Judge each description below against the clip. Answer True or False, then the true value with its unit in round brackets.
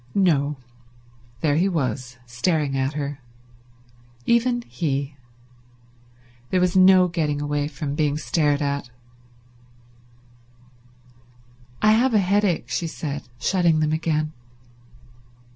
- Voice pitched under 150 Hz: False (155 Hz)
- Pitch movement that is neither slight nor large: True (4.2 semitones)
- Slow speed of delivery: True (105 wpm)